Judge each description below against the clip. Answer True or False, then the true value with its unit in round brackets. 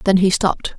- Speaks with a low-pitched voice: False (190 Hz)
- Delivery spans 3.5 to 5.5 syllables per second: False (6.3 syllables/s)